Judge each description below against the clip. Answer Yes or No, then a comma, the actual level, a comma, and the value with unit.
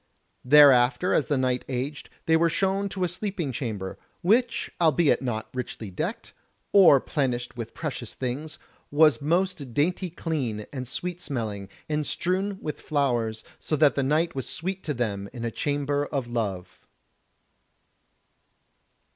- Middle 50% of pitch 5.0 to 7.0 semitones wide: Yes, wide, 5.4 semitones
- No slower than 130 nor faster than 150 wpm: Yes, average, 145 wpm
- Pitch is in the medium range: Yes, medium, 145 Hz